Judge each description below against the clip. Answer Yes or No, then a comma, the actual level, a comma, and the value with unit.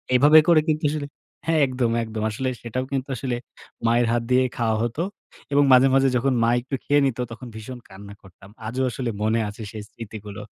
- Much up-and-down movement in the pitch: No, average, 3.4 semitones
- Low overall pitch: Yes, low, 120 Hz